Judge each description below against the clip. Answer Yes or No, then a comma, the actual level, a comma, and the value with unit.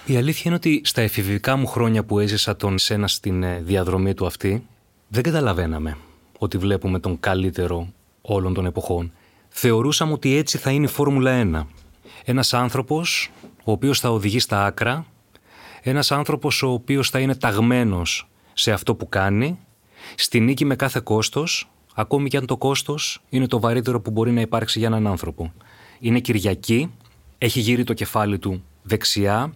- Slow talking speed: No, average, 160 wpm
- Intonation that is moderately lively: Yes, average, 4.8 semitones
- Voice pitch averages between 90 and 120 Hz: Yes, low, 115 Hz